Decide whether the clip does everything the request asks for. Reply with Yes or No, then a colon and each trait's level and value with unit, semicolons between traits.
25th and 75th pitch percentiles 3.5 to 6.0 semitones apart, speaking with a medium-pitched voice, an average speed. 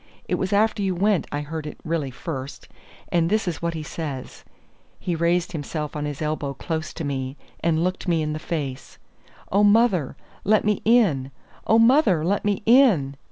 Yes: average, 5.3 semitones; medium, 165 Hz; average, 185 wpm